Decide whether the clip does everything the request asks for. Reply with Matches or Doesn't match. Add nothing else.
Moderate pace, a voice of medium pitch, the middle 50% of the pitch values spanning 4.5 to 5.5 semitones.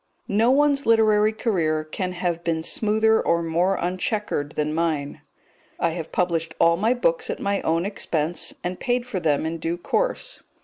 Matches